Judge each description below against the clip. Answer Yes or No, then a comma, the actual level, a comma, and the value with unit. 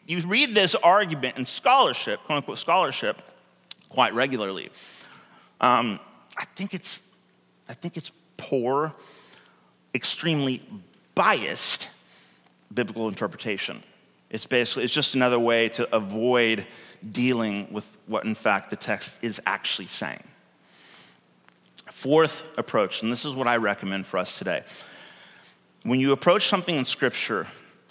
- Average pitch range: No, wide, 6.2 semitones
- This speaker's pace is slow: Yes, slow, 125 wpm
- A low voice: Yes, low, 125 Hz